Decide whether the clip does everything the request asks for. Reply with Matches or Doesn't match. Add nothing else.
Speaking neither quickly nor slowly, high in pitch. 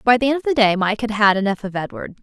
Doesn't match